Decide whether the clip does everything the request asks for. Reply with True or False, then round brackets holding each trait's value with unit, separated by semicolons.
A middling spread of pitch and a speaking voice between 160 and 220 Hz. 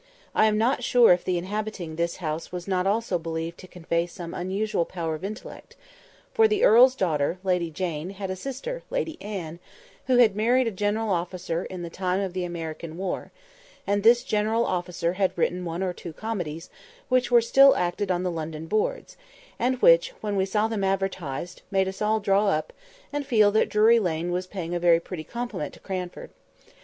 True (4.0 semitones; 190 Hz)